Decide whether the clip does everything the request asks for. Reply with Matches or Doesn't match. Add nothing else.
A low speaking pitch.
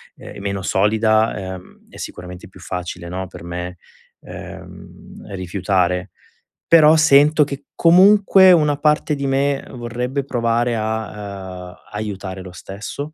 Matches